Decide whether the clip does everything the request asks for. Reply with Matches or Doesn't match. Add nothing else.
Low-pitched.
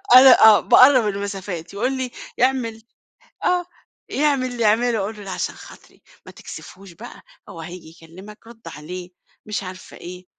Doesn't match